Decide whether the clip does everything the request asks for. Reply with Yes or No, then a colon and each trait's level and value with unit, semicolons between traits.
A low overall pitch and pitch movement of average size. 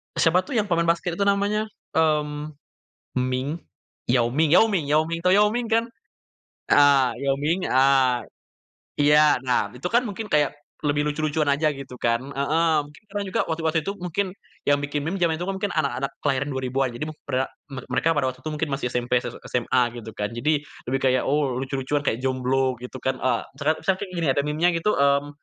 No: medium, 145 Hz; average, 3.9 semitones